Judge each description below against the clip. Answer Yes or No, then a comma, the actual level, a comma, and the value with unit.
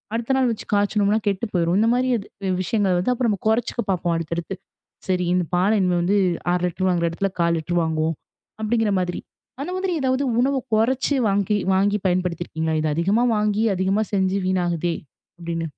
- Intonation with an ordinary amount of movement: Yes, average, 3.8 semitones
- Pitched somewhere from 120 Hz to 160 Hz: No, high, 190 Hz